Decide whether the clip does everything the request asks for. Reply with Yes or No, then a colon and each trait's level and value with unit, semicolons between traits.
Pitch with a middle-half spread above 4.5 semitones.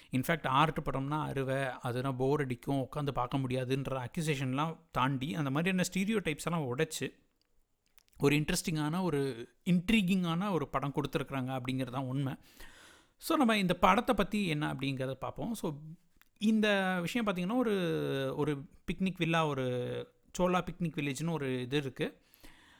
Yes: average, 4.9 semitones